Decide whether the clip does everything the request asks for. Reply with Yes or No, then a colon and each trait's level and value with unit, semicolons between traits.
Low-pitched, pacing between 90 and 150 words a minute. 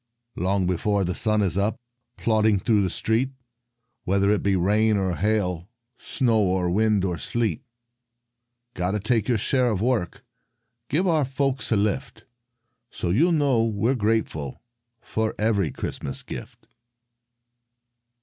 Yes: low, 105 Hz; average, 140 wpm